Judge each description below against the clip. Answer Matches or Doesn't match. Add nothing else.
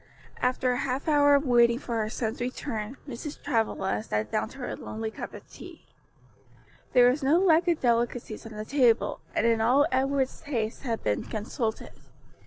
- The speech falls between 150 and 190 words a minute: Matches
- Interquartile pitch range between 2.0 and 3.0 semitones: Doesn't match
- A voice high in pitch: Matches